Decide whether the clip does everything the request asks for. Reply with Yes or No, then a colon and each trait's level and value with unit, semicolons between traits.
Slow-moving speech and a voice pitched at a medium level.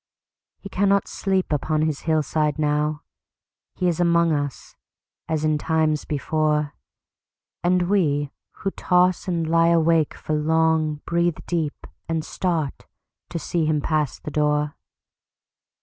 Yes: slow, 115 wpm; medium, 155 Hz